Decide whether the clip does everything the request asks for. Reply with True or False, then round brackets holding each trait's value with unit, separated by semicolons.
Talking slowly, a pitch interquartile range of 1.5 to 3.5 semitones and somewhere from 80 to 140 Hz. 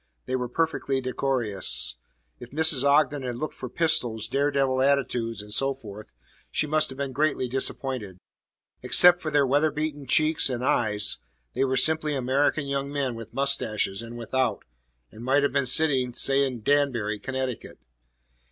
False (160 wpm; 2.8 semitones; 135 Hz)